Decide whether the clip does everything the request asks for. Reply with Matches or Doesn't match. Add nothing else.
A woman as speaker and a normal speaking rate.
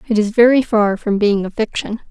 Doesn't match